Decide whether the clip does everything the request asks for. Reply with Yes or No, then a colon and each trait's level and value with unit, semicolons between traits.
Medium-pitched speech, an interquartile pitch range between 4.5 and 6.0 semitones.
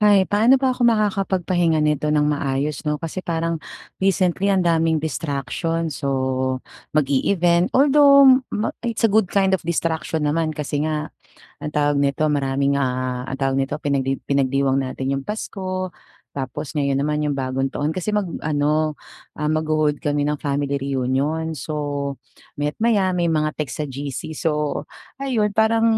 Yes: medium, 150 Hz; average, 4.8 semitones